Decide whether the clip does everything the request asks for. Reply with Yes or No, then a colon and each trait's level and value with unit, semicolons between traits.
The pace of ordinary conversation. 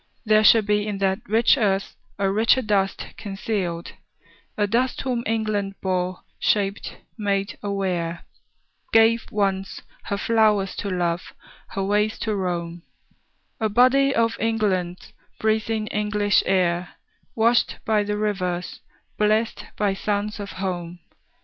No: slow, 125 wpm